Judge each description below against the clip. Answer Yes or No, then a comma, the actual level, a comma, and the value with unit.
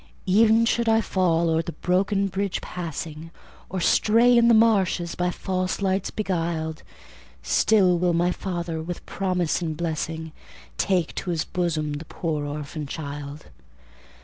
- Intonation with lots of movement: No, average, 3.2 semitones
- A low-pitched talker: No, medium, 175 Hz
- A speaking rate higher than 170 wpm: No, average, 145 wpm